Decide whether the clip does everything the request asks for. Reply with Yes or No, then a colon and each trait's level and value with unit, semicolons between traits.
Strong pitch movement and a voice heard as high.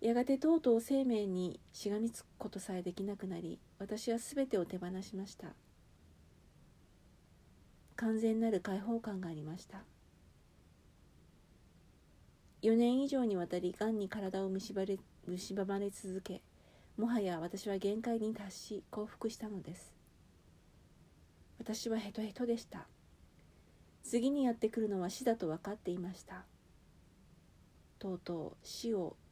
No: average, 3.9 semitones; high, 200 Hz